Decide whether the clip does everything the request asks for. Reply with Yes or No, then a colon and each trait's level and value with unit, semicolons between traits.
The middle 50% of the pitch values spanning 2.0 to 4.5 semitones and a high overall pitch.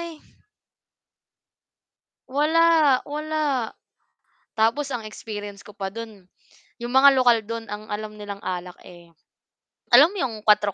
No: average, 5.3 semitones; high, 230 Hz